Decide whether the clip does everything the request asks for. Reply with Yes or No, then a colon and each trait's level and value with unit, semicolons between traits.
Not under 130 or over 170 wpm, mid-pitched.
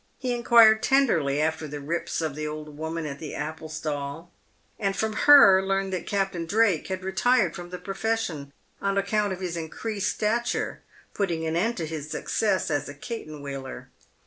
No: average, 180 wpm; medium, 175 Hz